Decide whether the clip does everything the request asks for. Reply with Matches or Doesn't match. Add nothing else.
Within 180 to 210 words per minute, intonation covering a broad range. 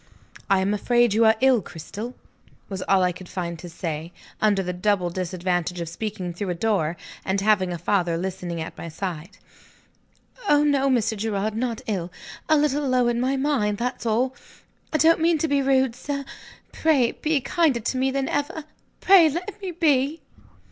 Matches